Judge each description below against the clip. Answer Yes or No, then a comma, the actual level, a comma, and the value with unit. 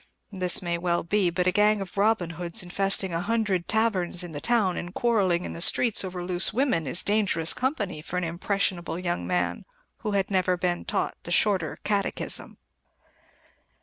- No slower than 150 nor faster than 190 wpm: Yes, average, 180 wpm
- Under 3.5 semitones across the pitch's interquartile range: Yes, average, 3.0 semitones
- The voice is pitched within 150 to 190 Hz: Yes, medium, 185 Hz